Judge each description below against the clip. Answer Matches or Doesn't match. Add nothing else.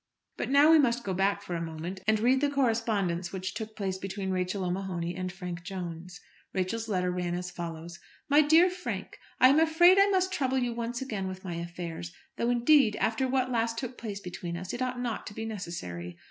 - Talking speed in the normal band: Doesn't match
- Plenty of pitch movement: Matches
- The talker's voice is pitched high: Matches